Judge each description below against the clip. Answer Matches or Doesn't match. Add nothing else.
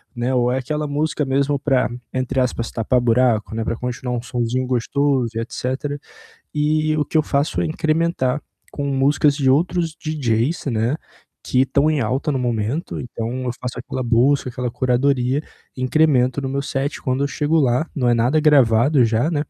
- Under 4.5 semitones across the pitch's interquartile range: Matches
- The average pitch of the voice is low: Matches